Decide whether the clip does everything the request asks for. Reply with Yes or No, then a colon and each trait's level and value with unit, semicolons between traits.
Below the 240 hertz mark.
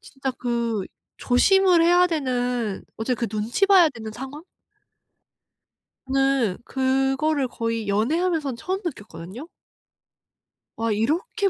No: very high, 265 Hz